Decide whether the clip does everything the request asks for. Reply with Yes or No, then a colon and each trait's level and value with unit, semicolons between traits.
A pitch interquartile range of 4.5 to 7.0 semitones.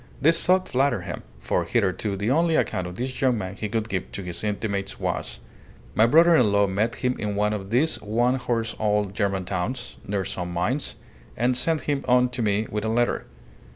No: average, 4.1 semitones